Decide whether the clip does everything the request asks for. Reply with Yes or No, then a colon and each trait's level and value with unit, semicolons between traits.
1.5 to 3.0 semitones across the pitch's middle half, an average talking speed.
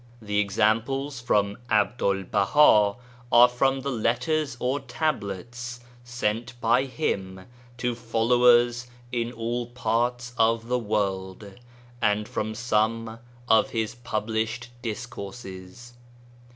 No: narrow, 2.5 semitones; slow, 100 wpm